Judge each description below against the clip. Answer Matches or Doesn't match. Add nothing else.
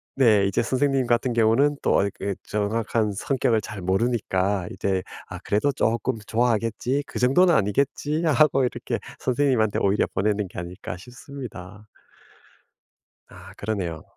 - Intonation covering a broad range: Doesn't match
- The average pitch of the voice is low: Matches